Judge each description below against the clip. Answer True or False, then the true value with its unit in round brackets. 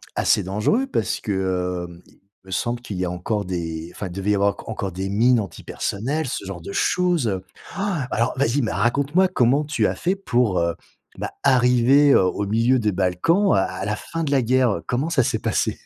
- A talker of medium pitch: False (110 Hz)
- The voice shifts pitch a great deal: True (6.4 semitones)